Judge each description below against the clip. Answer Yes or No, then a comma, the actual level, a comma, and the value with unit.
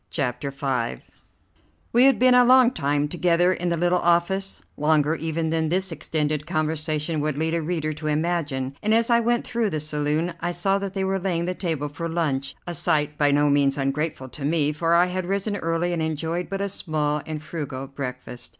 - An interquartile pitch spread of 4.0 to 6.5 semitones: No, average, 3.2 semitones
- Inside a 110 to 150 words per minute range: No, fast, 205 wpm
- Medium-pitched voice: Yes, medium, 160 Hz